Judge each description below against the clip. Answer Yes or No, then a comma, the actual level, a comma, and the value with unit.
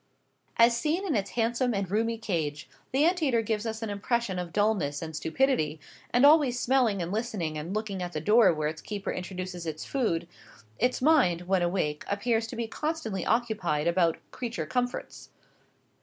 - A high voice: Yes, high, 210 Hz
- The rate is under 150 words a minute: No, average, 175 wpm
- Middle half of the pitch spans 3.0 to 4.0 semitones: No, wide, 5.5 semitones